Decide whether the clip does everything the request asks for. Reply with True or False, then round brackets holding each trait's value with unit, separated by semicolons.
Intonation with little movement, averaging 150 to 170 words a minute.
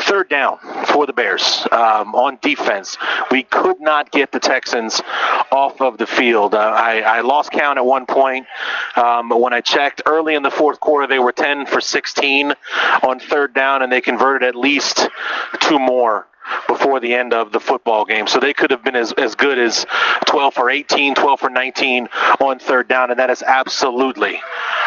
False (2.0 semitones; 195 wpm)